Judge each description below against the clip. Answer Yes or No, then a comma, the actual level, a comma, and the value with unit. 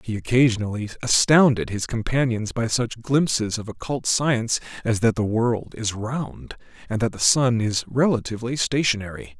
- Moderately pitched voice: No, low, 115 Hz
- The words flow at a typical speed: Yes, average, 155 wpm